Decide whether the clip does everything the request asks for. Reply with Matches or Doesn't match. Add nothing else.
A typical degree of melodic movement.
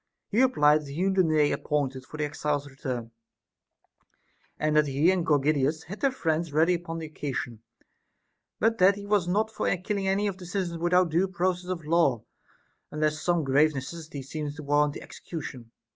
Matches